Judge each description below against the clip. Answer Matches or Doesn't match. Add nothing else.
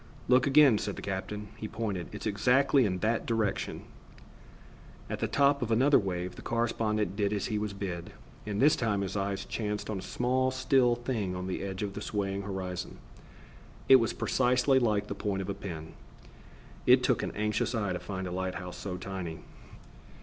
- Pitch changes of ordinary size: Matches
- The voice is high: Doesn't match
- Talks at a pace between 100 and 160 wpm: Doesn't match